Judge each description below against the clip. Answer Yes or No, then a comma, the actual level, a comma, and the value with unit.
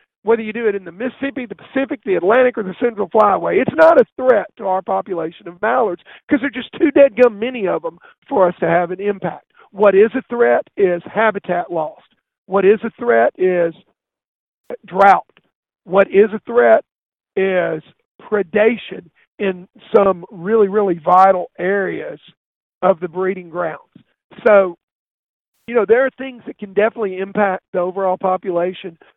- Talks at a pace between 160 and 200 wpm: Yes, average, 170 wpm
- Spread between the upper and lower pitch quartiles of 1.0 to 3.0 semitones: No, average, 4.2 semitones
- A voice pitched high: Yes, high, 200 Hz